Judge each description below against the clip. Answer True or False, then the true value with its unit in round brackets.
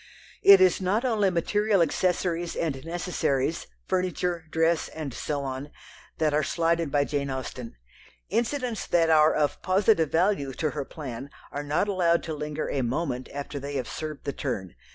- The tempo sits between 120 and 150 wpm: False (165 wpm)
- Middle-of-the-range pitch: True (160 Hz)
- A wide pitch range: False (4.2 semitones)